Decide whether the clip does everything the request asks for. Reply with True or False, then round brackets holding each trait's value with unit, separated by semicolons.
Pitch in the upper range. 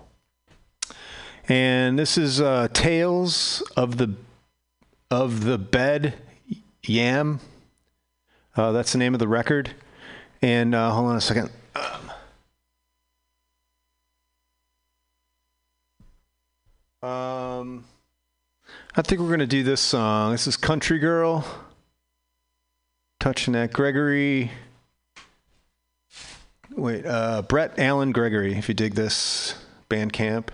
False (115 Hz)